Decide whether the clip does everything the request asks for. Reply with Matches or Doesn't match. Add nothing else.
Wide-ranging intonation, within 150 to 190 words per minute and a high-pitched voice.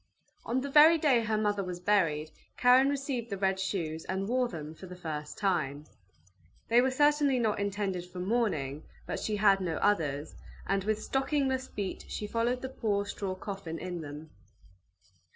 Matches